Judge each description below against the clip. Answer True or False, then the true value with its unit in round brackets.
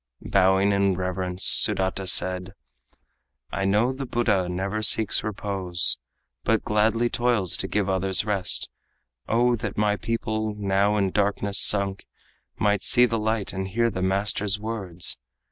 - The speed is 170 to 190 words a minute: False (145 wpm)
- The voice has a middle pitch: False (100 Hz)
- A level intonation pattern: True (2.3 semitones)